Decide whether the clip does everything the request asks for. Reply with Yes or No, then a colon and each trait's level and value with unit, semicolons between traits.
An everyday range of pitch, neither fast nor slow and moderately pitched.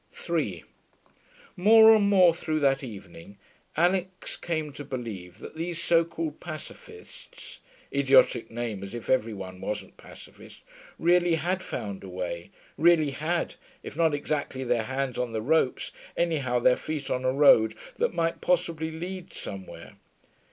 No: wide, 6.5 semitones; average, 145 wpm; medium, 145 Hz